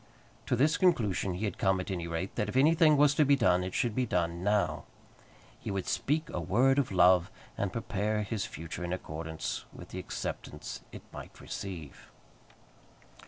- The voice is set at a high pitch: No, low, 100 Hz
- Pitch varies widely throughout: Yes, wide, 6.3 semitones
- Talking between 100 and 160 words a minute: No, average, 180 wpm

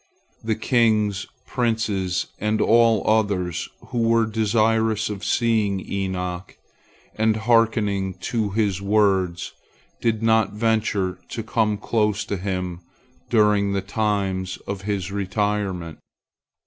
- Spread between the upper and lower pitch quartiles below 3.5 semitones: Yes, narrow, 2.5 semitones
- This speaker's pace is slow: Yes, slow, 110 wpm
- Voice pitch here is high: No, low, 105 Hz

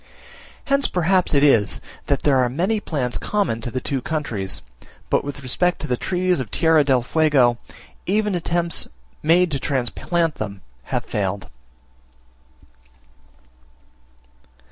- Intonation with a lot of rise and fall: Yes, wide, 6.2 semitones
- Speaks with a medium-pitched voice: Yes, medium, 145 Hz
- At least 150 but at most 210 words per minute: No, slow, 135 wpm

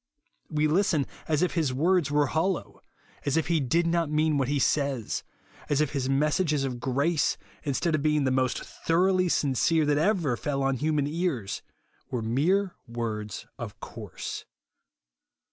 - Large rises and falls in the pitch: No, average, 3.6 semitones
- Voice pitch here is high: No, medium, 150 Hz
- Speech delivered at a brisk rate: No, average, 160 wpm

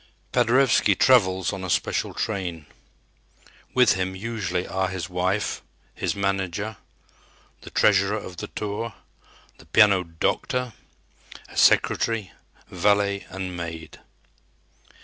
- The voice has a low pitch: Yes, very low, 95 Hz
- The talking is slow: Yes, slow, 110 wpm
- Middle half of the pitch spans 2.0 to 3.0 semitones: Yes, narrow, 2.5 semitones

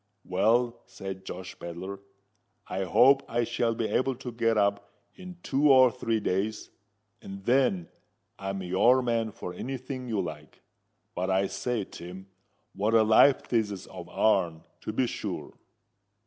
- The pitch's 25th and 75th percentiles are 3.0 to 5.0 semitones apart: Yes, average, 4.3 semitones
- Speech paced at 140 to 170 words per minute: Yes, average, 155 wpm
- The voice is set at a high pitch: No, low, 110 Hz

